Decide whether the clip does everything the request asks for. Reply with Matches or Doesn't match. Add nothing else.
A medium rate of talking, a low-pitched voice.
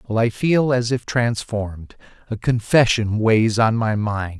Matches